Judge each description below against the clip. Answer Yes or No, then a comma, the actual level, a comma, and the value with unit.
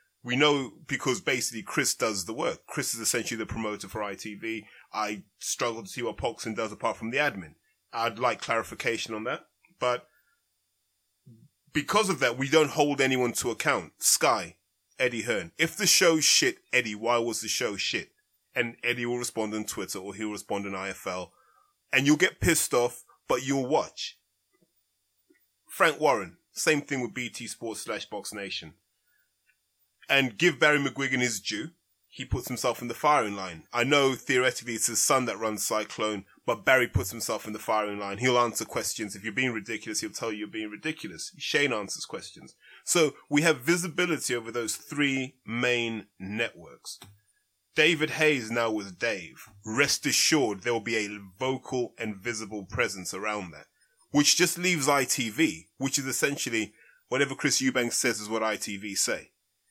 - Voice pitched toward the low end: Yes, low, 120 Hz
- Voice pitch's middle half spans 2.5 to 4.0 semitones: No, average, 4.8 semitones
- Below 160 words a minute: No, average, 170 wpm